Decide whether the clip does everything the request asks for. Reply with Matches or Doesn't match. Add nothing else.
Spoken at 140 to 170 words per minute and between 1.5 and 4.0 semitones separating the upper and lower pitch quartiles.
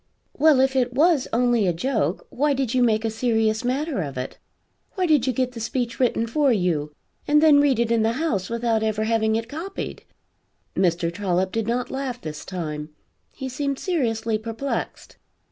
Doesn't match